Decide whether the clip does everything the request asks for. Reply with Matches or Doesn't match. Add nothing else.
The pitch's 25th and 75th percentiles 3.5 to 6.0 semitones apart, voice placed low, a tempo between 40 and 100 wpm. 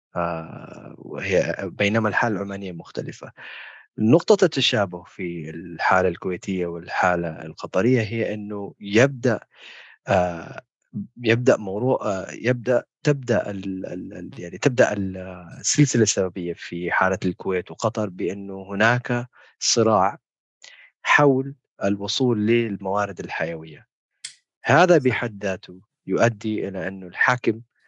Matches